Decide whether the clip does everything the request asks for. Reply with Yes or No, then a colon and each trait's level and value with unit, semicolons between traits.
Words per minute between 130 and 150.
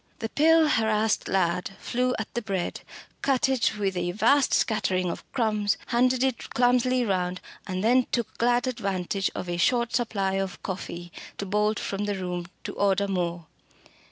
No: average, 165 wpm